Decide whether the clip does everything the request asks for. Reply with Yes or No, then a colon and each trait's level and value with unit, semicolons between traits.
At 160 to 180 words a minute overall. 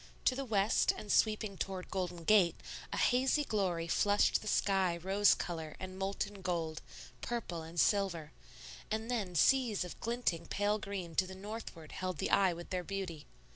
Yes: average, 170 wpm